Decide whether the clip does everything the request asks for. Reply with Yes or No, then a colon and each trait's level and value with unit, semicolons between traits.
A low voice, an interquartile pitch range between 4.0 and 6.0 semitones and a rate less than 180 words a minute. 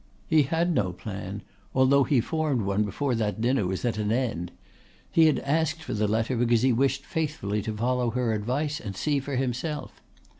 No: low, 125 Hz; average, 5.2 semitones; average, 190 wpm